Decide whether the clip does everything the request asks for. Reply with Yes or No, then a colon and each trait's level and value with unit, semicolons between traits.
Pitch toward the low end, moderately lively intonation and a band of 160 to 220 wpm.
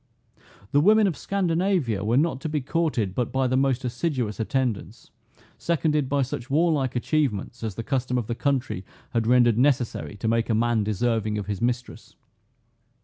Yes: low, 125 Hz; average, 4.2 semitones; average, 170 wpm